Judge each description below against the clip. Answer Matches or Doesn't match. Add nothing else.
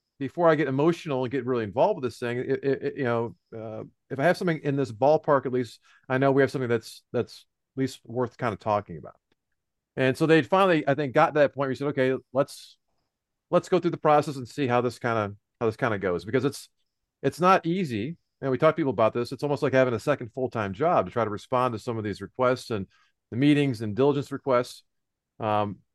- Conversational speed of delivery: Doesn't match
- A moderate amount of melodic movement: Matches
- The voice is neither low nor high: Doesn't match